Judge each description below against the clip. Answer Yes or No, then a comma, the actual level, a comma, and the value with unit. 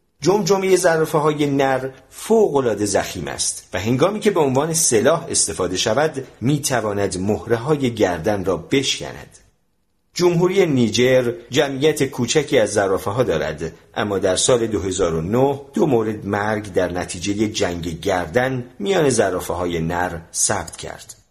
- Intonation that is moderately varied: No, wide, 6.9 semitones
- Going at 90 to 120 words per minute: No, average, 130 wpm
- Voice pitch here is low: Yes, low, 120 Hz